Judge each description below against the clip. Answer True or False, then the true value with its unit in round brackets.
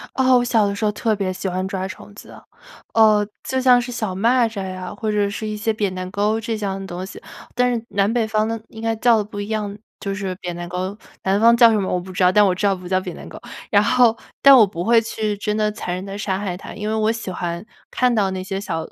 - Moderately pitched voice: False (205 Hz)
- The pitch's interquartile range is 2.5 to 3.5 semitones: True (2.9 semitones)